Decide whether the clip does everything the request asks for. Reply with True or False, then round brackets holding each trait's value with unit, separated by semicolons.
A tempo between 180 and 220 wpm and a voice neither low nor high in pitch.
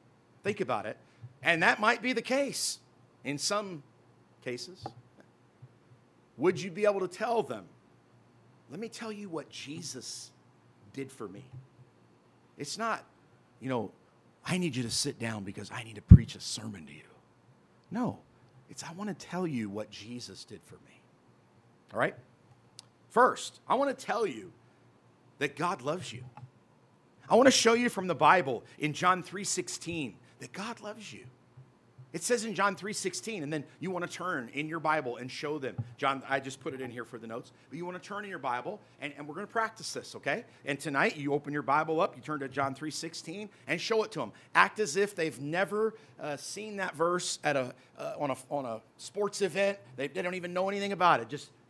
True (200 wpm; 150 Hz)